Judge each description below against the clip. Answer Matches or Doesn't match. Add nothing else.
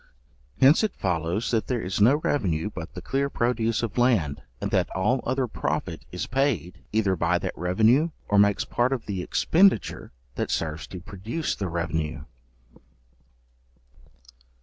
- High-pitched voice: Doesn't match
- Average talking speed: Matches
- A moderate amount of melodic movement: Doesn't match